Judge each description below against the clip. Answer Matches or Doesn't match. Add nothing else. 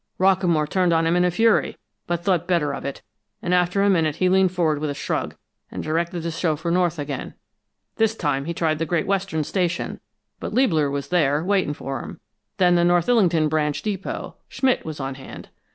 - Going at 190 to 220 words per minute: Matches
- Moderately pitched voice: Matches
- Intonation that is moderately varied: Matches